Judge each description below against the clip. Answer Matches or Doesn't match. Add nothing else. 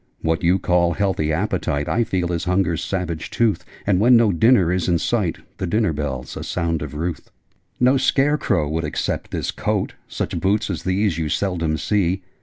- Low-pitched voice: Matches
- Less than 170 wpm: Doesn't match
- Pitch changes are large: Doesn't match